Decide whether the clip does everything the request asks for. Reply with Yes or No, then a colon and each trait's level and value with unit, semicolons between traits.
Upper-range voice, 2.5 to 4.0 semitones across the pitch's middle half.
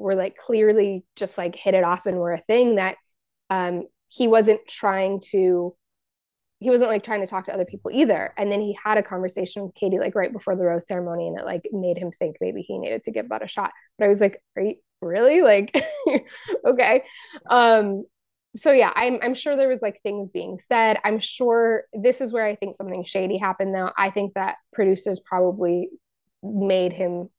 Yes: high, 200 Hz; average, 3.3 semitones